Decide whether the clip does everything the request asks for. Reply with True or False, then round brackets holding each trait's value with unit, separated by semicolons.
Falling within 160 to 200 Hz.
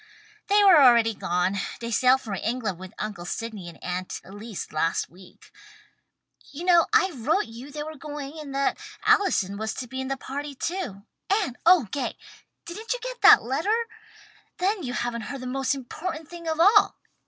False (270 Hz)